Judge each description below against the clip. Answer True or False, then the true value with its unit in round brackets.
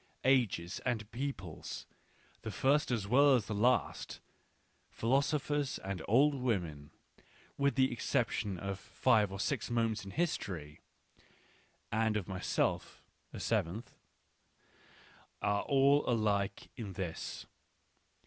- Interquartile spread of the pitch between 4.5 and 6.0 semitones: True (5.4 semitones)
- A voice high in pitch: False (110 Hz)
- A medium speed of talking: False (115 wpm)